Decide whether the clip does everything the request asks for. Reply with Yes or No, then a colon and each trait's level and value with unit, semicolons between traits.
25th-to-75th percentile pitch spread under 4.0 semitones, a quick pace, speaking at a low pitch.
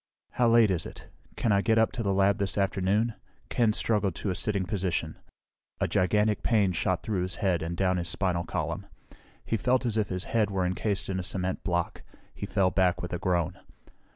Yes: average, 2.8 semitones; fast, 210 wpm; very low, 95 Hz